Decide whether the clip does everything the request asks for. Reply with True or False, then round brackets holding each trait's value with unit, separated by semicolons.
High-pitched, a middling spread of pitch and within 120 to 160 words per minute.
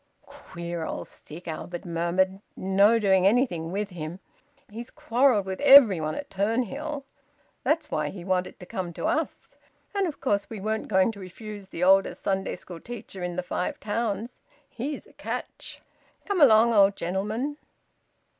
True (200 Hz; 4.3 semitones; 155 wpm)